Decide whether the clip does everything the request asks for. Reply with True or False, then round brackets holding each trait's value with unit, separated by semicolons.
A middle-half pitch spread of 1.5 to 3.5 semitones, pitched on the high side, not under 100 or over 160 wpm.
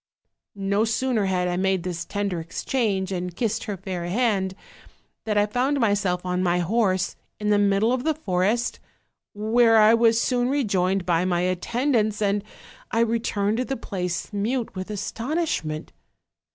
False (3.9 semitones; 205 Hz; 155 wpm)